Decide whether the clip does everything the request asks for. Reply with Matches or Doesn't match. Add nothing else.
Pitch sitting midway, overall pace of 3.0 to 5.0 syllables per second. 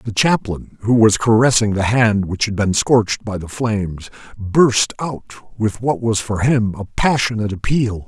Doesn't match